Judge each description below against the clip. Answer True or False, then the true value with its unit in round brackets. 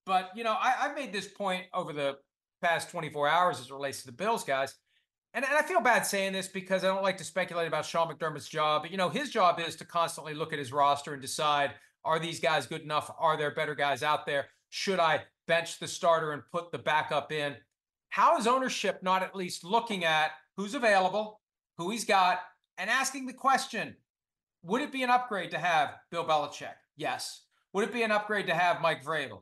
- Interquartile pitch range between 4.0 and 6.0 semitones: True (4.5 semitones)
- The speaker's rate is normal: False (220 wpm)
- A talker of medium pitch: True (170 Hz)